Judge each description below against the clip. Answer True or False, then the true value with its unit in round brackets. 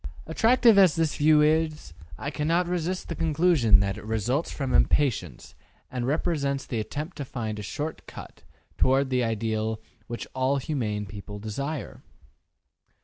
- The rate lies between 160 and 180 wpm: False (145 wpm)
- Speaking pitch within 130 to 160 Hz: True (140 Hz)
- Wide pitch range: True (6.1 semitones)